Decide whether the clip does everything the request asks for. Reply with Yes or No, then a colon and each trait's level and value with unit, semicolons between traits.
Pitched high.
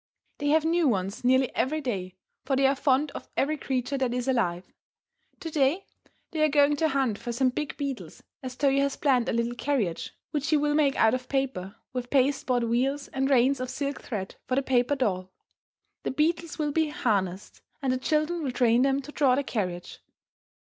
Yes: very high, 265 Hz